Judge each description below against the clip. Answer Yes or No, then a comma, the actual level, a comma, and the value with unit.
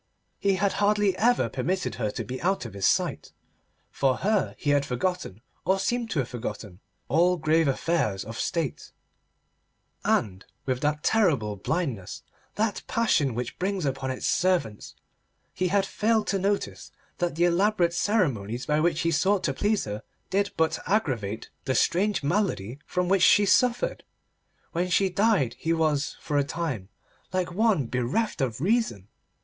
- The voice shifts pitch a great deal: Yes, wide, 7.2 semitones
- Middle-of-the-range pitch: Yes, medium, 165 Hz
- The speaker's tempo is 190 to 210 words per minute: No, average, 155 wpm